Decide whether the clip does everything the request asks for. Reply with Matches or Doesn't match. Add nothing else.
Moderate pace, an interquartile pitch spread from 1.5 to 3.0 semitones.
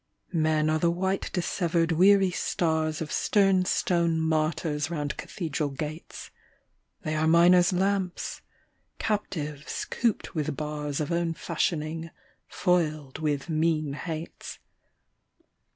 Doesn't match